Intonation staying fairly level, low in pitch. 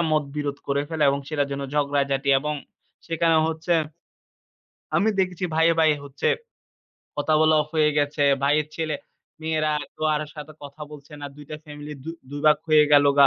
No: narrow, 1.6 semitones; medium, 150 Hz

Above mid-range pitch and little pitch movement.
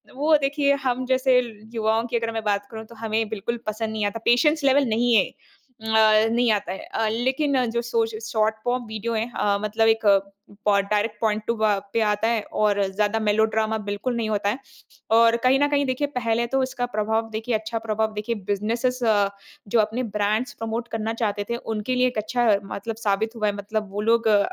Yes: high, 225 Hz; narrow, 2.1 semitones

